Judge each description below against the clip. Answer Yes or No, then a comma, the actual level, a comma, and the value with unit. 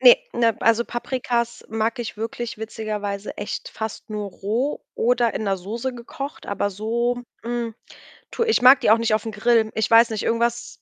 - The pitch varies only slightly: Yes, narrow, 1.8 semitones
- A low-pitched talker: No, high, 230 Hz